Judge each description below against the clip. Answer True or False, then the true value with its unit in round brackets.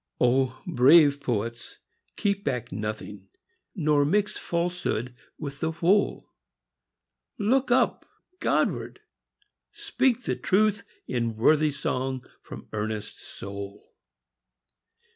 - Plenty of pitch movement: True (7.4 semitones)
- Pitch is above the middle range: False (140 Hz)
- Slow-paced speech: True (95 wpm)